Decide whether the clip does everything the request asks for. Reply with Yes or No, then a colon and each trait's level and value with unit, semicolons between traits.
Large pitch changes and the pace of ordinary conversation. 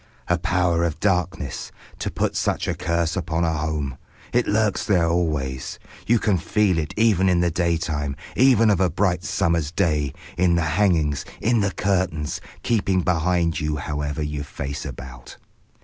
No: average, 3.7 semitones; average, 165 wpm